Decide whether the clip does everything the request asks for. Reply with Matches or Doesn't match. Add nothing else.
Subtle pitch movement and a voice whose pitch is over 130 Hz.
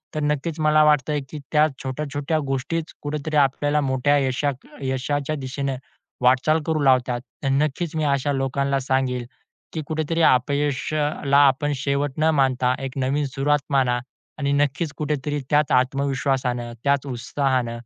Matches